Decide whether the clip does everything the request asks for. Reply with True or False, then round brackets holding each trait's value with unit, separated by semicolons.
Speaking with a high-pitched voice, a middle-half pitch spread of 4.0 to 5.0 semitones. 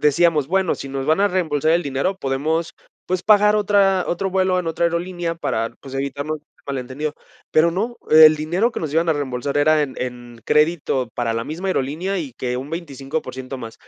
False (155 Hz; 4.7 semitones)